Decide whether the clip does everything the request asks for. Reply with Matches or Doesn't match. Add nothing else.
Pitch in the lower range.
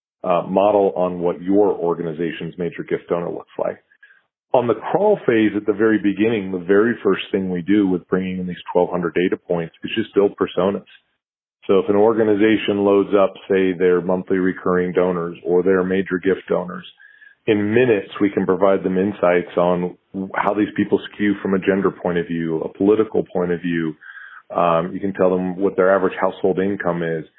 Matches